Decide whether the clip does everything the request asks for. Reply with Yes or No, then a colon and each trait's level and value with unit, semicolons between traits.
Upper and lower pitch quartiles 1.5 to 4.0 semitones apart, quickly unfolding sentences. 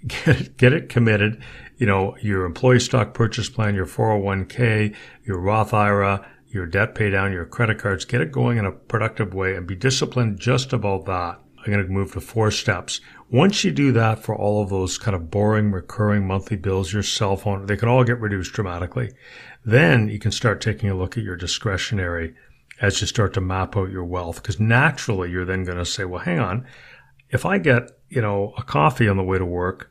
Yes: average, 3.7 semitones; fast, 215 wpm